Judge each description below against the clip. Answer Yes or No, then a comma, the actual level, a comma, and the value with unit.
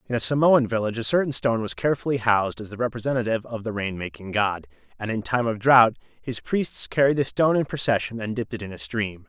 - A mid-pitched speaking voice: No, low, 115 Hz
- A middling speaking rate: No, fast, 235 wpm